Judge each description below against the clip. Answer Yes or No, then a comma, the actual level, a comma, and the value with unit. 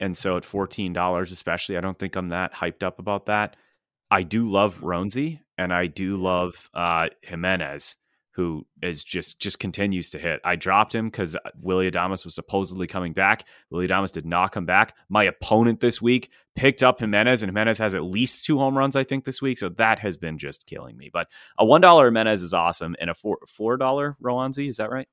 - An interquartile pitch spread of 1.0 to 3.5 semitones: No, average, 4.3 semitones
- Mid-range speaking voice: No, very low, 95 Hz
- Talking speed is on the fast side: Yes, fast, 210 wpm